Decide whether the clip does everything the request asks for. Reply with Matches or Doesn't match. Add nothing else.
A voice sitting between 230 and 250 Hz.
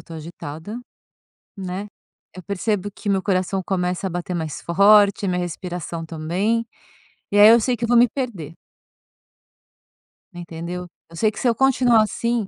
Doesn't match